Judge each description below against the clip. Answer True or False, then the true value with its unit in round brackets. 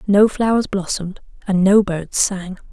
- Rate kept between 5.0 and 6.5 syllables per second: False (4.5 syllables/s)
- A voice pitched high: True (195 Hz)